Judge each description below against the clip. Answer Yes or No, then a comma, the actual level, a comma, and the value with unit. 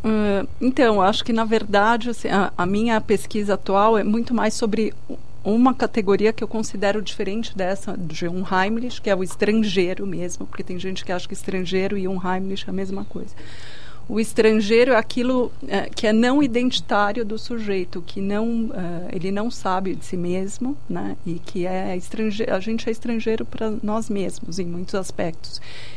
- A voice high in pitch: Yes, high, 205 Hz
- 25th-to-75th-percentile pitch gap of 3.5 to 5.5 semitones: No, average, 3.0 semitones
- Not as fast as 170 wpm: No, fast, 185 wpm